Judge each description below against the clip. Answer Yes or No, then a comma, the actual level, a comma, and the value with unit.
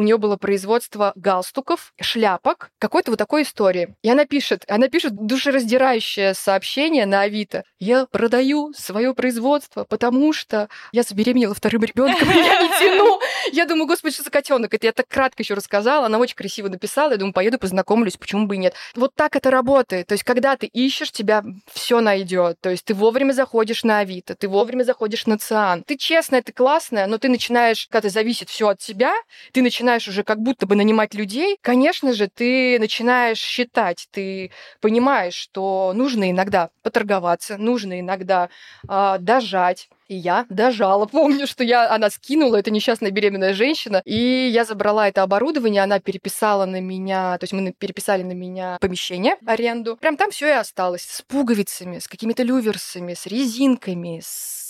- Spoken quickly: Yes, fast, 175 wpm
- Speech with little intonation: No, average, 4.7 semitones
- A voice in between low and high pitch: No, high, 225 Hz